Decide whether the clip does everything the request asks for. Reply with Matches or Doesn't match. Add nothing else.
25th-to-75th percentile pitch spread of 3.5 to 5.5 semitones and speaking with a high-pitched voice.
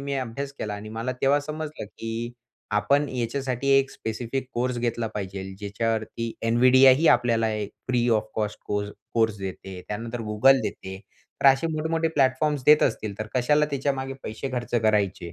Doesn't match